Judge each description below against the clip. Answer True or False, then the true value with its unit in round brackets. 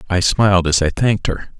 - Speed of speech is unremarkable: False (225 wpm)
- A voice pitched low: True (95 Hz)